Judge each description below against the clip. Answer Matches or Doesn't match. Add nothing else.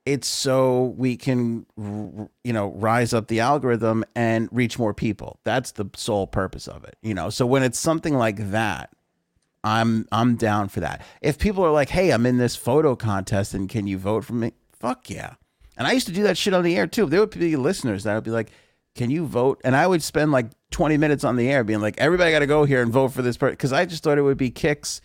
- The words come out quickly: Matches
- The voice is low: Matches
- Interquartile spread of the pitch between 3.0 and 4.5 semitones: Doesn't match